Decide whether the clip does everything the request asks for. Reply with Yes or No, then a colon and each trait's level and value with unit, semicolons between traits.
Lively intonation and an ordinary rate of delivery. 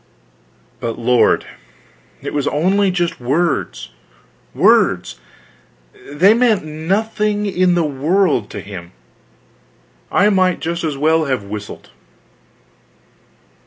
No: wide, 6.1 semitones; slow, 100 wpm